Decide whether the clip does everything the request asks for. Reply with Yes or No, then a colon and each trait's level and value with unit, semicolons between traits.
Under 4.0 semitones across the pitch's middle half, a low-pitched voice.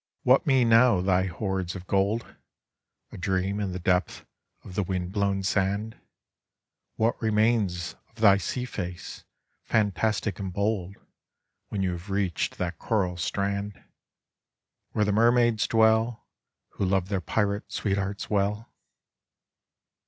Yes: average, 2.8 semitones; low, 100 Hz